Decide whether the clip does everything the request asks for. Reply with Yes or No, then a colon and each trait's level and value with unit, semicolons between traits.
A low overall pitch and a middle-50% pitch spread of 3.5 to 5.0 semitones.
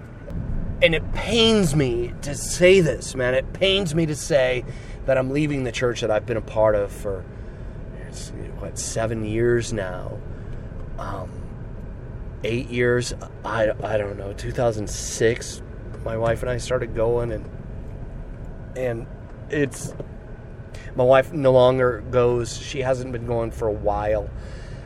No: low, 120 Hz; average, 3.1 semitones